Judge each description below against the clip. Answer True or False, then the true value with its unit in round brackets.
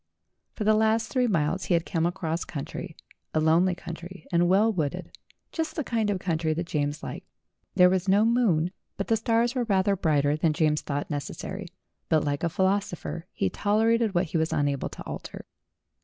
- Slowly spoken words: False (185 wpm)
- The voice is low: False (180 Hz)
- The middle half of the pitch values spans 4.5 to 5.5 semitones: True (4.9 semitones)